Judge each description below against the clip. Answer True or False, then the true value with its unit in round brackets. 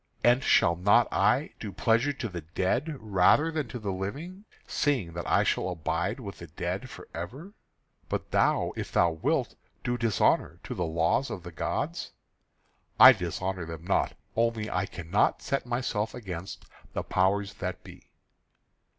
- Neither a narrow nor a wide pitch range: False (6.0 semitones)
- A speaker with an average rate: True (160 wpm)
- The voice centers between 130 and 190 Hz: False (100 Hz)